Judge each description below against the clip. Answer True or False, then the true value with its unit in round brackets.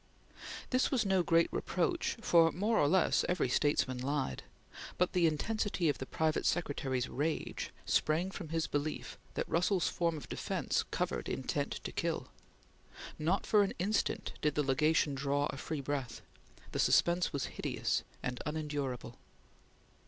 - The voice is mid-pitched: True (155 Hz)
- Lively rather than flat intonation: False (3.9 semitones)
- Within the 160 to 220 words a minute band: False (150 wpm)